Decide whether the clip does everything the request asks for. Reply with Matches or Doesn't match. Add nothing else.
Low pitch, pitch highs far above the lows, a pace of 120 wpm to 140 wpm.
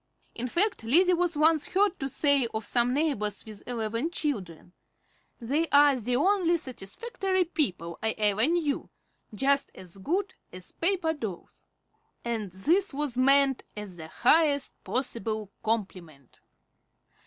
Doesn't match